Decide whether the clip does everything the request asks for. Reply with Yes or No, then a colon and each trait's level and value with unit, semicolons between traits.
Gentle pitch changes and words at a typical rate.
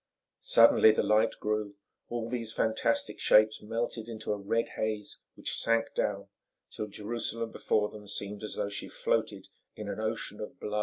Yes: narrow, 1.4 semitones; average, 175 wpm